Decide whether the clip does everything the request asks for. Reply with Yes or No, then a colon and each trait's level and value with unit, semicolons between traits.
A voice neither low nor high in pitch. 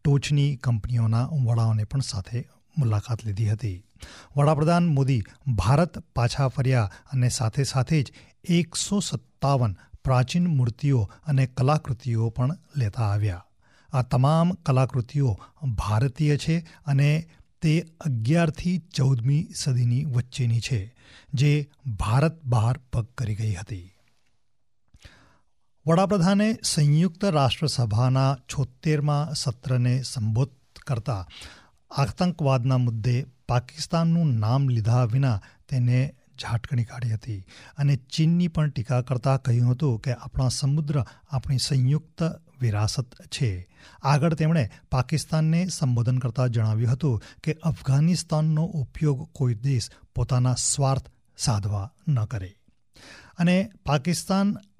No: low, 130 Hz